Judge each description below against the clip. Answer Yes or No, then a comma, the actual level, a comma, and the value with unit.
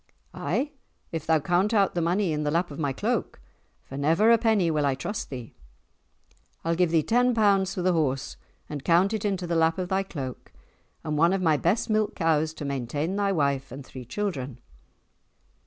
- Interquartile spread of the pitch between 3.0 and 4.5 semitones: No, average, 5.1 semitones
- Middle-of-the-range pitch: Yes, medium, 165 Hz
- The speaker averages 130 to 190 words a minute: No, average, 200 wpm